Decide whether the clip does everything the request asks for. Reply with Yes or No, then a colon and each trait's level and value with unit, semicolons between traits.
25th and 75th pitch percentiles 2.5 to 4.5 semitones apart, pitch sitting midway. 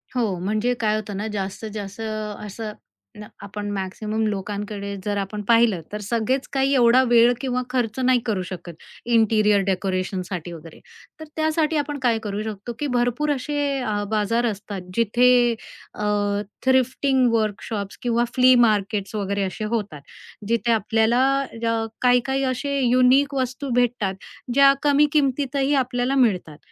No: average, 3.7 semitones; high, 225 Hz